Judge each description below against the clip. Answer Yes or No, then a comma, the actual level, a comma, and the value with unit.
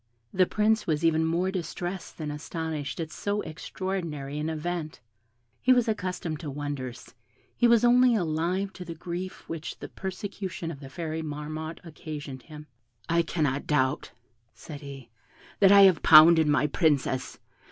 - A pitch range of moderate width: Yes, average, 3.7 semitones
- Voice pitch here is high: No, medium, 160 Hz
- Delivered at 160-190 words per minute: No, average, 150 wpm